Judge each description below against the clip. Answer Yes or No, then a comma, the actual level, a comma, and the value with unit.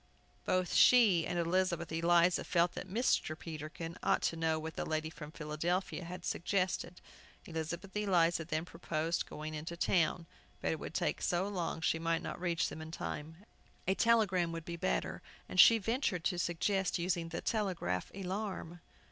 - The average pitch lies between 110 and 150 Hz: No, medium, 170 Hz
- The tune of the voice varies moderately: No, narrow, 2.3 semitones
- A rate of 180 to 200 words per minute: No, average, 165 wpm